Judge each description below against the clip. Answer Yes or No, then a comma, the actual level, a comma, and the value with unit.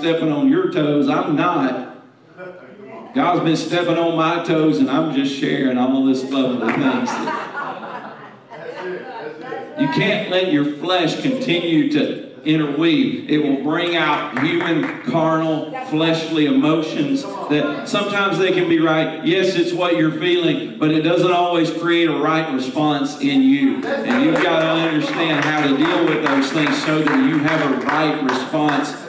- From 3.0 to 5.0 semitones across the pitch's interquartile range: Yes, average, 4.0 semitones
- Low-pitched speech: No, medium, 165 Hz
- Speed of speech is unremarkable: Yes, average, 160 wpm